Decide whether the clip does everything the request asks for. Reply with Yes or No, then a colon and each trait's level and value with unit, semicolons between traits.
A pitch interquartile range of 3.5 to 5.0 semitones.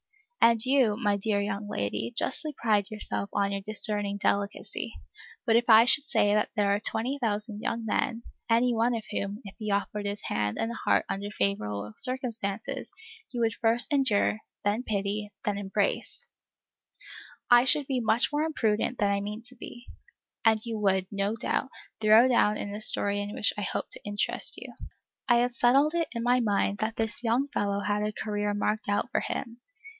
No: average, 2.7 semitones